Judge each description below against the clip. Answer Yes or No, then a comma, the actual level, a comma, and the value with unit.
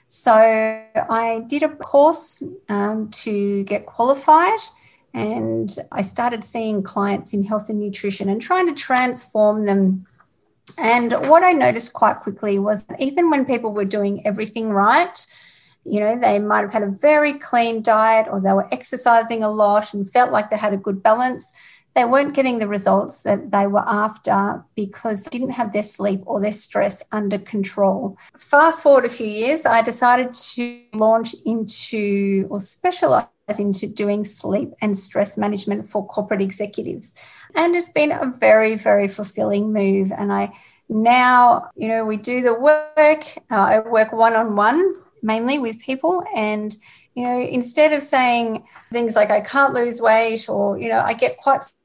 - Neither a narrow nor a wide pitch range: Yes, average, 3.7 semitones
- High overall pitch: Yes, high, 220 Hz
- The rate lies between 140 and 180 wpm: Yes, average, 170 wpm